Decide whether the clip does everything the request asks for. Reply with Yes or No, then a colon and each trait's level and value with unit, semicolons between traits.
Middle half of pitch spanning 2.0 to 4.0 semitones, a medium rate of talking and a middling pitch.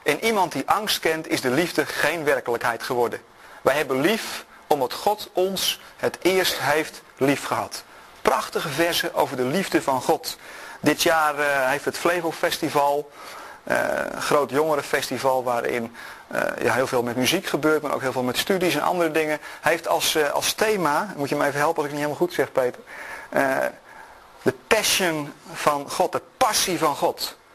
Yes: average, 3.6 semitones; average, 170 wpm; medium, 150 Hz